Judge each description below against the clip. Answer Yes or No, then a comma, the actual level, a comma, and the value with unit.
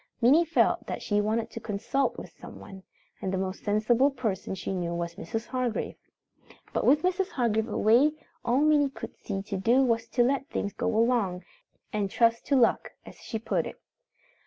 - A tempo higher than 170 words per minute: Yes, average, 185 wpm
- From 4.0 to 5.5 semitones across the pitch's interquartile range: Yes, average, 4.4 semitones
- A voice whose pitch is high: Yes, high, 230 Hz